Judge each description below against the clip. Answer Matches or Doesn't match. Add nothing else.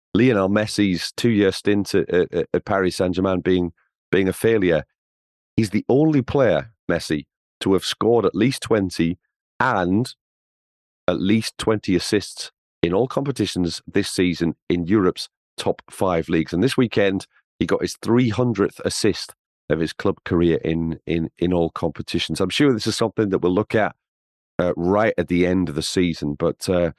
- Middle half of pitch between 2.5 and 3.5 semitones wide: Doesn't match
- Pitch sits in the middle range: Doesn't match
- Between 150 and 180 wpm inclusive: Matches